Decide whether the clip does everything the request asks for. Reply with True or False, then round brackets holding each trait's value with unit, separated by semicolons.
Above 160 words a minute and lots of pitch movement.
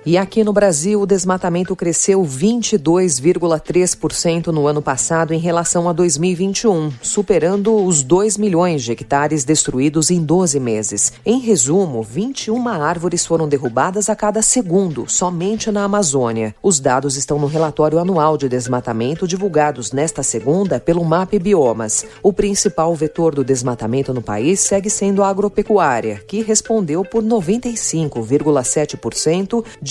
False (135 wpm; 5.7 semitones)